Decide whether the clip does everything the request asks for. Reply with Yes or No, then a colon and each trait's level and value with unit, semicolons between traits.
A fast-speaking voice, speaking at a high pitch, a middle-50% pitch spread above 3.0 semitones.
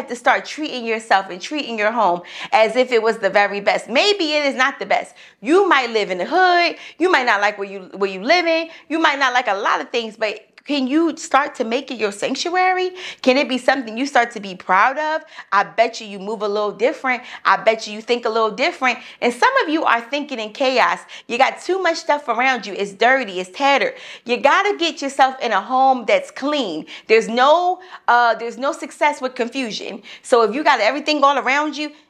Yes: fast, 230 wpm; very high, 260 Hz; average, 5.3 semitones